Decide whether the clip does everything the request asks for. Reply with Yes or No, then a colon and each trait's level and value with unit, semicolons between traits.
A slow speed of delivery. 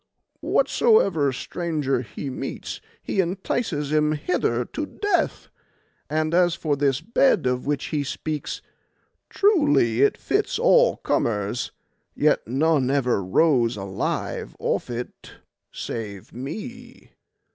Yes: slow, 115 wpm